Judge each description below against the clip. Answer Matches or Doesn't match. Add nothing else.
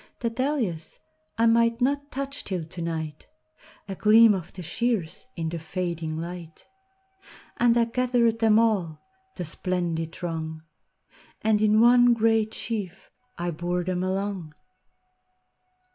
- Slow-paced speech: Matches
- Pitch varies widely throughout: Matches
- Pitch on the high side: Matches